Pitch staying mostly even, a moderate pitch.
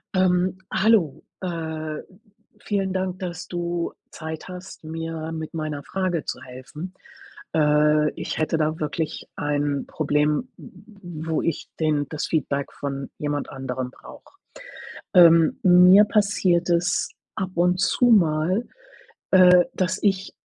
No: average, 3.3 semitones; medium, 165 Hz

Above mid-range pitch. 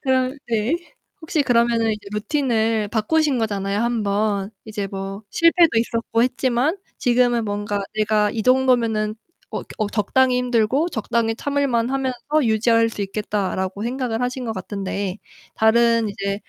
Yes: high, 230 Hz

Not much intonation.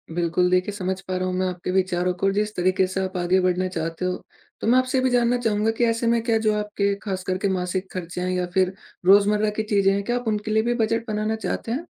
No: average, 3.2 semitones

